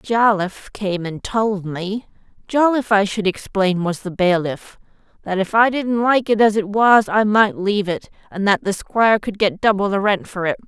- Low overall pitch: No, high, 205 Hz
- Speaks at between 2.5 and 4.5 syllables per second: No, 4.8 syllables/s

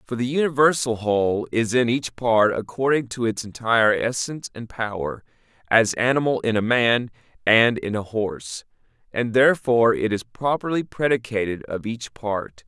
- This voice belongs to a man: Yes, male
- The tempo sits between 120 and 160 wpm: Yes, average, 155 wpm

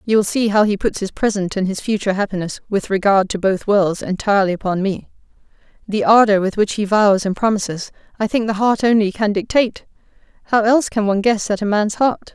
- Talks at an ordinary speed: No, fast, 215 wpm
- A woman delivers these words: Yes, female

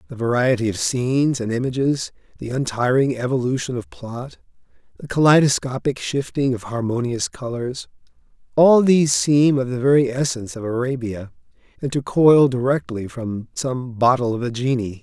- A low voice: Yes, low, 125 Hz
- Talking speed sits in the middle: Yes, average, 145 wpm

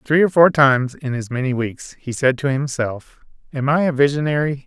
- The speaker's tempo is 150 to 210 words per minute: Yes, fast, 205 wpm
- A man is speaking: Yes, male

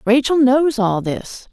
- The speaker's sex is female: Yes, female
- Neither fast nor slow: Yes, average, 160 wpm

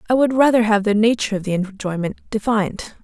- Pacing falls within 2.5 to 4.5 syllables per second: No, 6.3 syllables/s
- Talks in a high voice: Yes, high, 215 Hz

